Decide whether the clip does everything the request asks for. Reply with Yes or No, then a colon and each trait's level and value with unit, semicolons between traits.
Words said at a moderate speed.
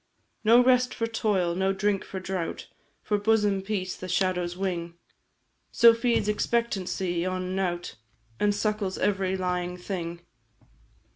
No: slow, 130 wpm